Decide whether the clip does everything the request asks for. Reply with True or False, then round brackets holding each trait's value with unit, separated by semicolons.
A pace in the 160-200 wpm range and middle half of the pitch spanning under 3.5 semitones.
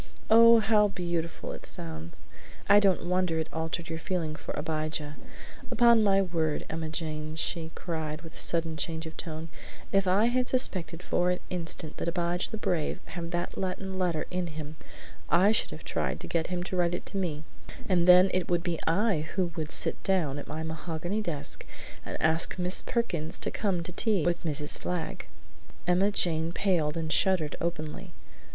True (185 wpm; 2.7 semitones)